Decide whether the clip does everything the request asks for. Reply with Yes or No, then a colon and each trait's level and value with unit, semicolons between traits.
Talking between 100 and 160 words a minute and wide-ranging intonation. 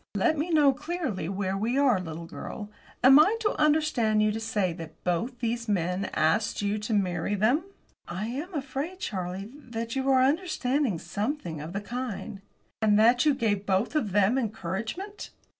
No: average, 175 wpm; wide, 5.9 semitones